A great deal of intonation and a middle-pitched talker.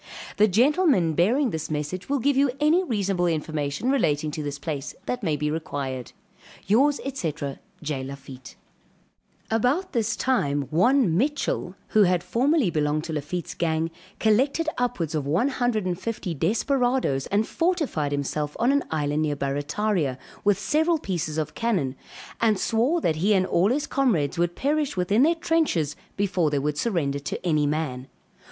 Yes: wide, 8.6 semitones; medium, 180 Hz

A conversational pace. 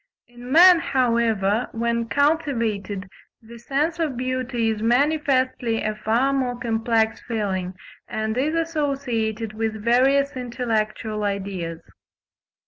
No: slow, 110 wpm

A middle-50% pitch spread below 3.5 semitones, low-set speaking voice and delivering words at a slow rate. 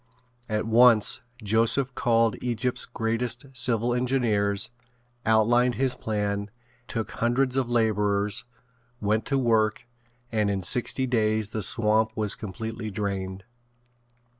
Yes: narrow, 2.5 semitones; low, 110 Hz; slow, 115 wpm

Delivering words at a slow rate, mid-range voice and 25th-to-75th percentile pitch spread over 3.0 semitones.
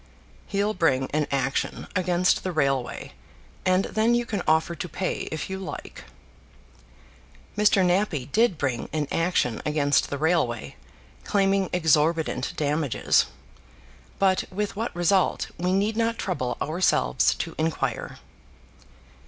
Yes: slow, 125 wpm; medium, 175 Hz; average, 4.6 semitones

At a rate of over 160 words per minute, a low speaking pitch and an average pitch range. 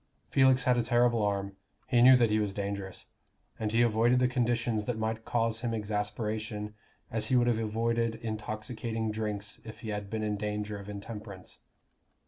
No: average, 175 wpm; low, 110 Hz; narrow, 2.0 semitones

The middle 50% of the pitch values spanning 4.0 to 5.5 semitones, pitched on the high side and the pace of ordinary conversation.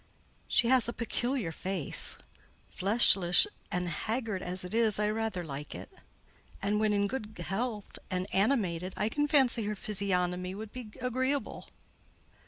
Yes: average, 4.3 semitones; high, 210 Hz; average, 145 wpm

